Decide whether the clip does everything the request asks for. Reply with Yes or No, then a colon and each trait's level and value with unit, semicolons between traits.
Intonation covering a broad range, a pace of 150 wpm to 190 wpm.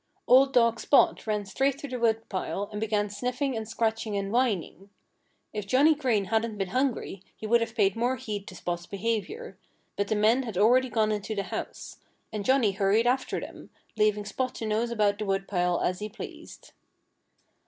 No: average, 3.2 semitones; average, 185 wpm